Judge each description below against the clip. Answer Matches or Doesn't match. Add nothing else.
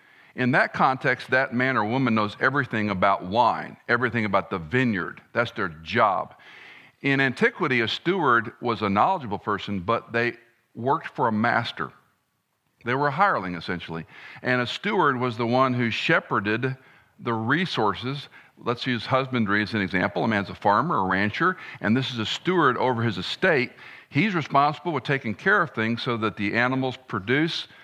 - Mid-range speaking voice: Doesn't match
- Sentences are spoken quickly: Doesn't match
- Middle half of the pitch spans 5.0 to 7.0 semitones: Doesn't match